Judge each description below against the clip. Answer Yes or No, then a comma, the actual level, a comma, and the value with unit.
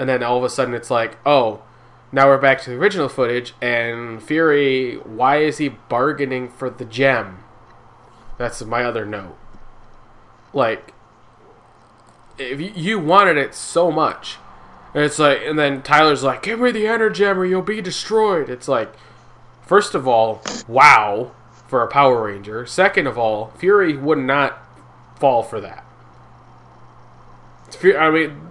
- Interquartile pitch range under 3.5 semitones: No, average, 5.1 semitones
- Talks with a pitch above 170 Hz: No, low, 135 Hz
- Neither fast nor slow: Yes, average, 155 wpm